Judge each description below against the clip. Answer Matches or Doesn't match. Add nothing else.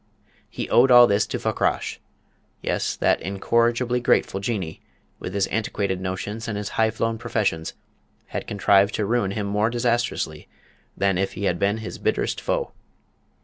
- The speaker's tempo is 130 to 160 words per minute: Matches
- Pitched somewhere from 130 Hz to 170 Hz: Doesn't match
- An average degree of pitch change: Matches